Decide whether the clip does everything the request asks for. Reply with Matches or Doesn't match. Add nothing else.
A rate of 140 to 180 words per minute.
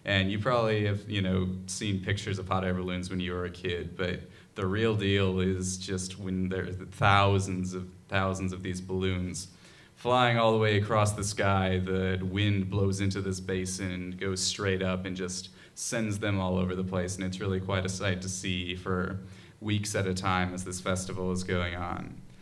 Doesn't match